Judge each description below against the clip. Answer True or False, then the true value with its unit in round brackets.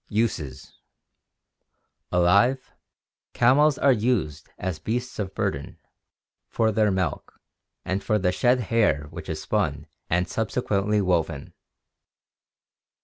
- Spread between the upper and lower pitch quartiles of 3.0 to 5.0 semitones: True (4.7 semitones)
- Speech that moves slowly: True (110 wpm)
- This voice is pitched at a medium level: False (100 Hz)